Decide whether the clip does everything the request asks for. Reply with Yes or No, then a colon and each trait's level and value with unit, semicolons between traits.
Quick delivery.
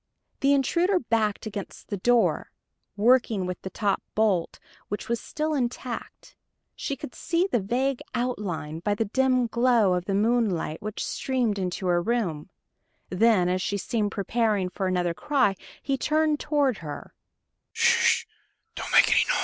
No: average, 140 wpm